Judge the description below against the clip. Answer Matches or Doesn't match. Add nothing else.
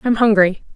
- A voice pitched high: Matches